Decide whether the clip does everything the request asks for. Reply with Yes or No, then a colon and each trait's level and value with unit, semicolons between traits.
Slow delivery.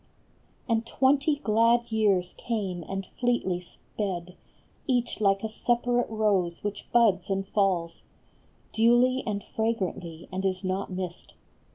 Yes: slow, 125 wpm